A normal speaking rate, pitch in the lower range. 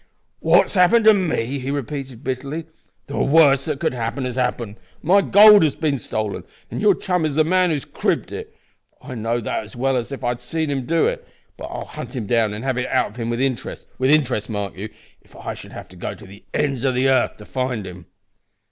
No: fast, 240 wpm; low, 130 Hz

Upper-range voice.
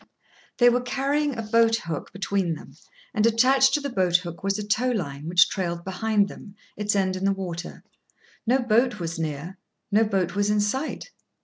Yes: high, 205 Hz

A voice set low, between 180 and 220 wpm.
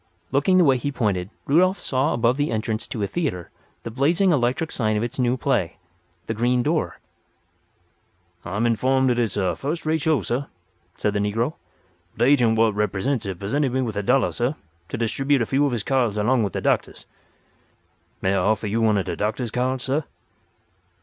Yes: low, 120 Hz; average, 195 wpm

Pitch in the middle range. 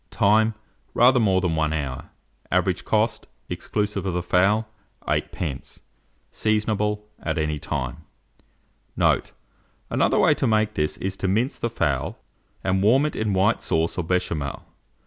No: very low, 95 Hz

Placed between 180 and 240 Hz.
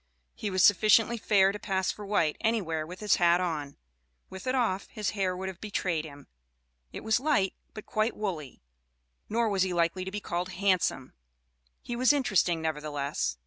Yes: high, 190 Hz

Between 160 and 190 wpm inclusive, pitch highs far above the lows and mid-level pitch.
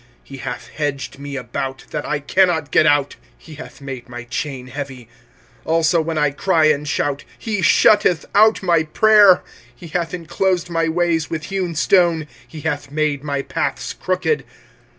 No: average, 175 wpm; average, 3.5 semitones; medium, 155 Hz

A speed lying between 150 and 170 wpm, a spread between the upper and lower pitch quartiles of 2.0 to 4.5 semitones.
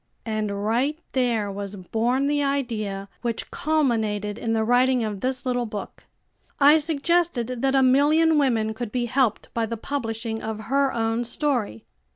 Yes: average, 160 wpm; average, 3.9 semitones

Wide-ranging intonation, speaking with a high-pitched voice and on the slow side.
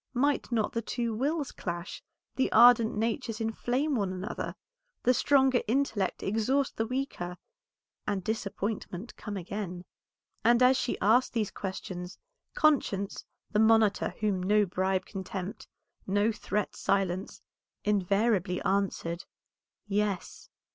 No: average, 3.8 semitones; high, 210 Hz; slow, 120 wpm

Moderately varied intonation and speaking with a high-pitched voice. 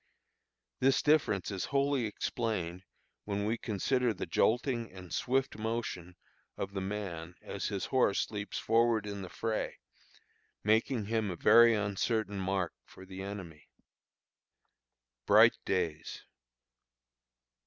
No: average, 3.5 semitones; low, 105 Hz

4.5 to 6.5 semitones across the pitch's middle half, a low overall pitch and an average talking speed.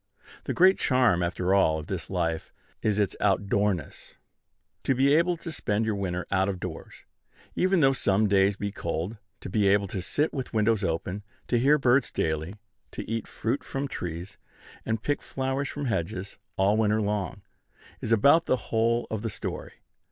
Yes: average, 5.2 semitones; low, 105 Hz; average, 175 wpm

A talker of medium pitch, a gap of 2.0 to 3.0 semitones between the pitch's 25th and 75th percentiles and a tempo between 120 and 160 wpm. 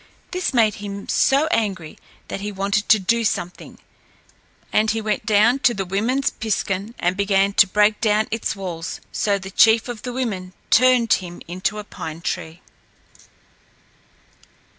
No: high, 210 Hz; average, 2.7 semitones; average, 155 wpm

